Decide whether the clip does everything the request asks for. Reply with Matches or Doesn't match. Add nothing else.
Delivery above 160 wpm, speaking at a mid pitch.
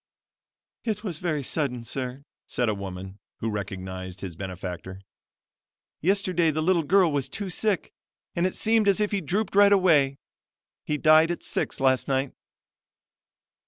Doesn't match